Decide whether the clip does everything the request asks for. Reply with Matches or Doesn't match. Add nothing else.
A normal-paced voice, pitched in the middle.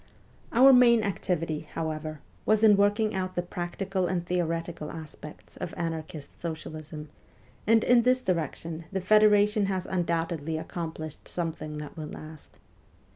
Doesn't match